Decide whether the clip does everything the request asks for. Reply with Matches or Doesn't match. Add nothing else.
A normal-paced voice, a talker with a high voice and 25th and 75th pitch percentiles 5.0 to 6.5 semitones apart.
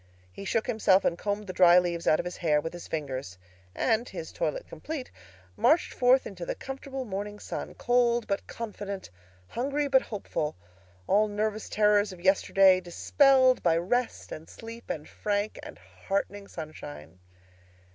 Matches